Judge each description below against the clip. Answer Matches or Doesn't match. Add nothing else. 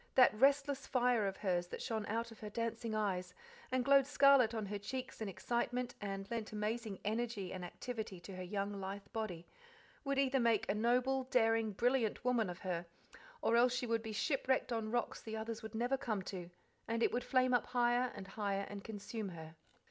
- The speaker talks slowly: Doesn't match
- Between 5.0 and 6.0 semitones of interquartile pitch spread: Doesn't match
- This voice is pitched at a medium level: Doesn't match